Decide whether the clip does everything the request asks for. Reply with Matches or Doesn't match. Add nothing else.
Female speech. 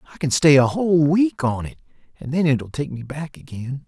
Doesn't match